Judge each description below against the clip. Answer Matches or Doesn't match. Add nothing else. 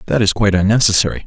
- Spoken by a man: Matches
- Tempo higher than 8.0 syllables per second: Matches